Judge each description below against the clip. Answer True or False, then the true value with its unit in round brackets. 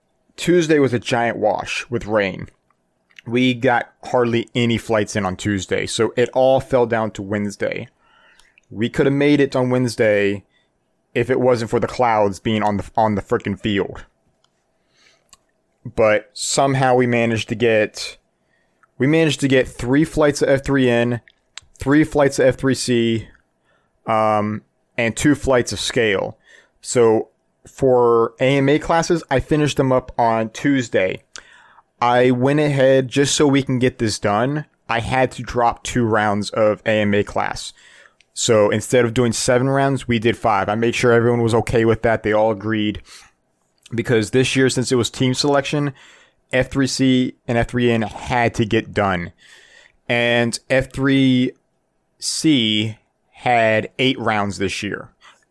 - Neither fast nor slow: True (150 wpm)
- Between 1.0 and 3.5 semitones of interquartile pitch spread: True (3.2 semitones)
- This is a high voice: False (120 Hz)